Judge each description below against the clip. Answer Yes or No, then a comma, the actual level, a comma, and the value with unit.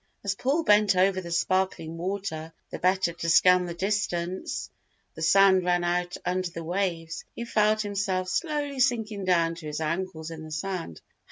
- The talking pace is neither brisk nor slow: Yes, average, 170 wpm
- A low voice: No, medium, 185 Hz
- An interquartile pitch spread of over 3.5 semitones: No, average, 3.0 semitones